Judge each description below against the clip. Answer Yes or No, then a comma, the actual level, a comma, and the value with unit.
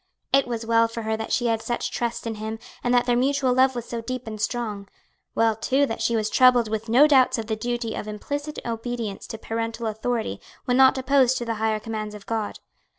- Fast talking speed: Yes, fast, 225 wpm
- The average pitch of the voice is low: No, high, 230 Hz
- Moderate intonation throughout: No, narrow, 2.2 semitones